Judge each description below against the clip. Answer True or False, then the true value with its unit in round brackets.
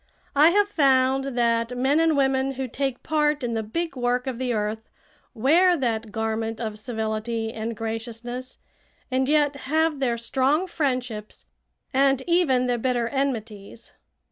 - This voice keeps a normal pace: True (145 wpm)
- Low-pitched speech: False (255 Hz)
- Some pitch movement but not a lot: True (3.5 semitones)